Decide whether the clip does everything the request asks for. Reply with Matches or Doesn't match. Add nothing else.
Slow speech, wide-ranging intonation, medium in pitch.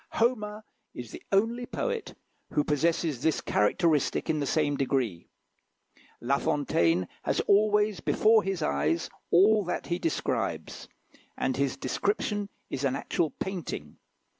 Matches